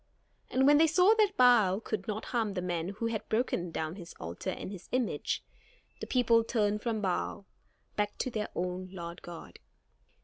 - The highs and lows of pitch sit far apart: No, average, 4.8 semitones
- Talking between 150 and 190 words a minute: Yes, average, 180 wpm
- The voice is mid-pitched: No, high, 210 Hz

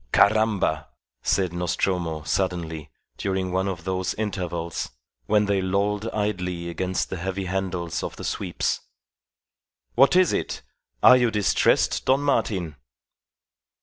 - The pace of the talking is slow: Yes, slow, 120 wpm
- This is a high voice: No, very low, 95 Hz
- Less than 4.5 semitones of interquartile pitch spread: Yes, average, 3.0 semitones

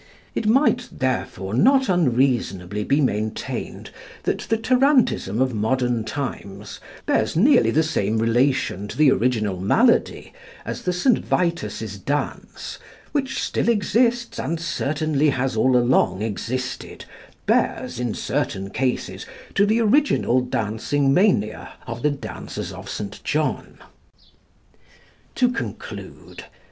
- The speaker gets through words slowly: Yes, slow, 120 wpm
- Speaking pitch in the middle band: No, low, 130 Hz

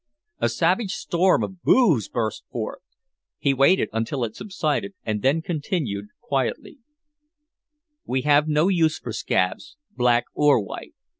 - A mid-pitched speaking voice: Yes, medium, 145 Hz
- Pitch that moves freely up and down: Yes, wide, 7.2 semitones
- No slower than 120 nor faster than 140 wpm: Yes, slow, 135 wpm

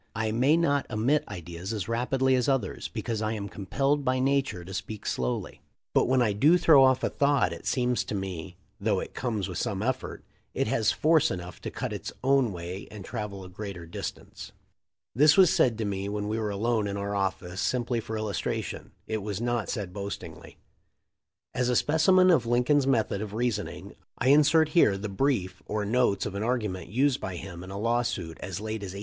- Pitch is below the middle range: Yes, low, 110 Hz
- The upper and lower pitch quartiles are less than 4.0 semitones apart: No, average, 4.8 semitones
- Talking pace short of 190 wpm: No, fast, 205 wpm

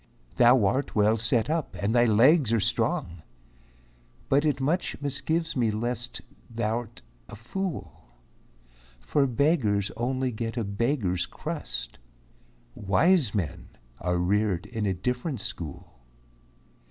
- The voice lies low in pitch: Yes, low, 120 Hz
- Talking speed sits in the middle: No, slow, 120 wpm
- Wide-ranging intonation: No, average, 4.7 semitones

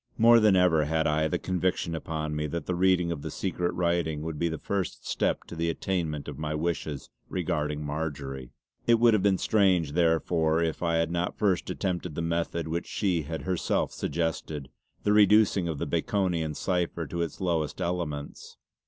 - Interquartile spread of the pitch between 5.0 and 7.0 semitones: No, average, 2.7 semitones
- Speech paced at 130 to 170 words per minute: No, average, 180 wpm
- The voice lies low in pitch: Yes, very low, 85 Hz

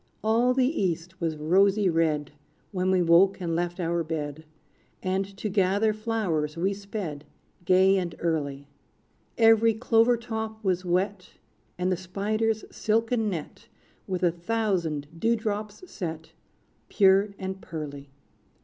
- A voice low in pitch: No, high, 190 Hz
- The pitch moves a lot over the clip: No, average, 4.3 semitones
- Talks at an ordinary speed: No, slow, 130 wpm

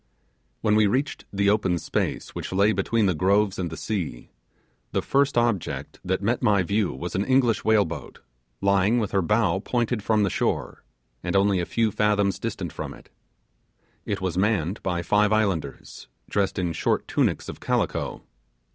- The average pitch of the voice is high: No, low, 100 Hz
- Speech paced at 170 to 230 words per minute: Yes, average, 175 wpm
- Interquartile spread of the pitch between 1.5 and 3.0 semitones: Yes, average, 2.7 semitones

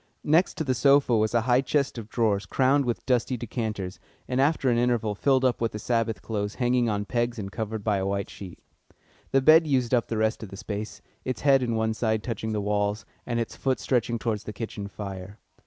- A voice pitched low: Yes, low, 115 Hz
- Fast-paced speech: Yes, fast, 220 wpm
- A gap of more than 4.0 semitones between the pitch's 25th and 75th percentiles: No, average, 3.3 semitones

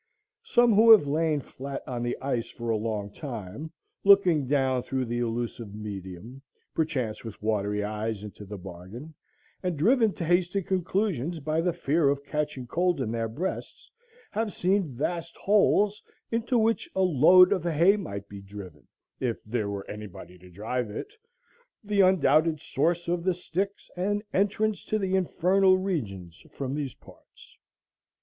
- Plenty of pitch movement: Yes, wide, 8.8 semitones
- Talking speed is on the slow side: No, average, 160 wpm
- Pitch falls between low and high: Yes, medium, 150 Hz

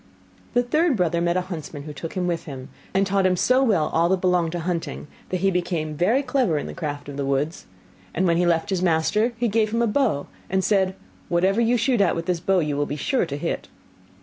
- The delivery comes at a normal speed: No, fast, 245 wpm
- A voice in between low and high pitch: Yes, medium, 180 Hz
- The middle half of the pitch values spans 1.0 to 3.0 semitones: No, average, 4.3 semitones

